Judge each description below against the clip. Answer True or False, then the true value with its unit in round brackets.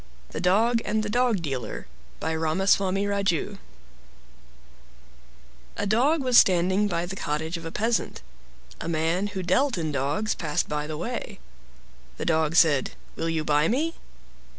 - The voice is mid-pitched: True (180 Hz)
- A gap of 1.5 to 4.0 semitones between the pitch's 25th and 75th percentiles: False (4.8 semitones)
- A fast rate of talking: False (150 wpm)